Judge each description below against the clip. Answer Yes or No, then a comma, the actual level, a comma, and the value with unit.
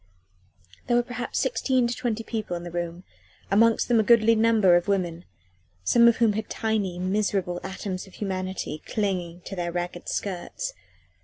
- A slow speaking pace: No, average, 165 wpm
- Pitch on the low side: No, high, 200 Hz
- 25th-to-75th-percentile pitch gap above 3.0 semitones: Yes, average, 4.3 semitones